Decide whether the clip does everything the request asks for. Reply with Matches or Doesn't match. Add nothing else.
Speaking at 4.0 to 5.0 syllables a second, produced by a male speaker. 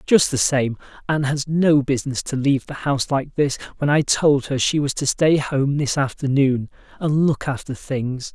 Matches